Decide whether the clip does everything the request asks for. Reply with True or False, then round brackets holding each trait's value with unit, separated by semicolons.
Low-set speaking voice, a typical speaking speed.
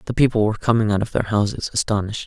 False (110 Hz; 240 wpm)